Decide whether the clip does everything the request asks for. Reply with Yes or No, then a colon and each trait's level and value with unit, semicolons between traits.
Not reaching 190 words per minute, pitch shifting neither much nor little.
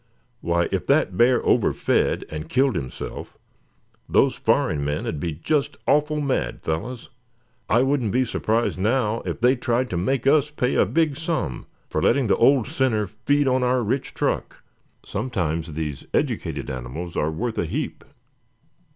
No: average, 155 wpm; wide, 7.8 semitones